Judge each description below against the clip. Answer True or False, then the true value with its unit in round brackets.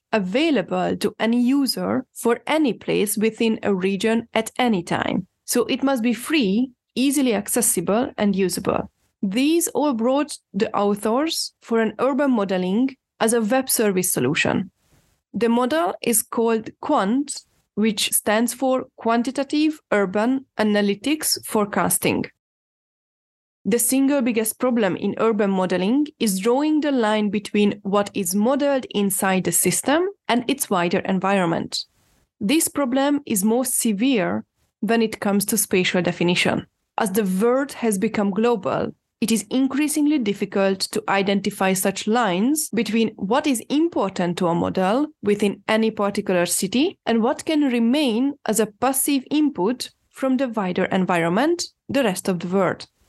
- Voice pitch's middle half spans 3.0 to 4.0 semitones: False (4.9 semitones)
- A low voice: False (225 Hz)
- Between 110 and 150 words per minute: True (140 wpm)